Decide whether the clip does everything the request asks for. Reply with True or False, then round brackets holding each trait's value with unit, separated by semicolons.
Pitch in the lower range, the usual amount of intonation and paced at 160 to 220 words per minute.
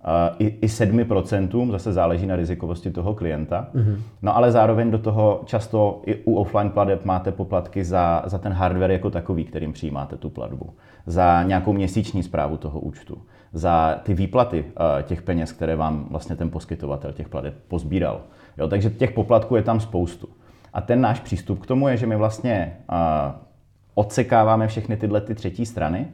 True (95 Hz; 4.5 semitones; 165 wpm)